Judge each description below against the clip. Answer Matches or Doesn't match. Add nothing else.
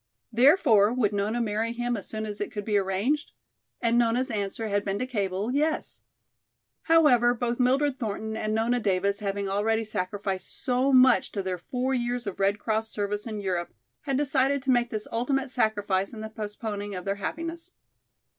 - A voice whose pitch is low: Doesn't match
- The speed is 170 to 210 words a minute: Matches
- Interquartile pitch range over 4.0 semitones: Doesn't match